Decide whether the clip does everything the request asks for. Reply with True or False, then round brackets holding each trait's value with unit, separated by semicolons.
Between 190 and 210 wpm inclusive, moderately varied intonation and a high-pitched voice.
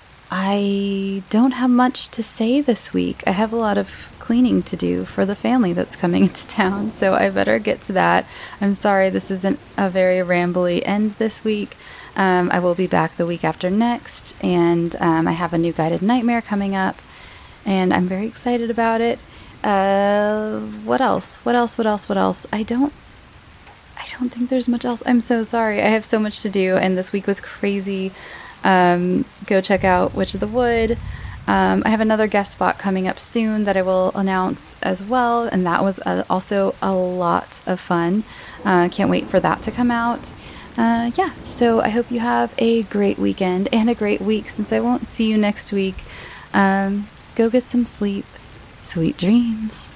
True (195 wpm; 3.7 semitones; 200 Hz)